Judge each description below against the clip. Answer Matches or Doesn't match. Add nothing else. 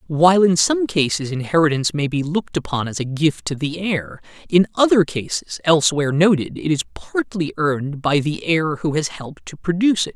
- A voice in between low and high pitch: Matches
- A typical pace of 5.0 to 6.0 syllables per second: Matches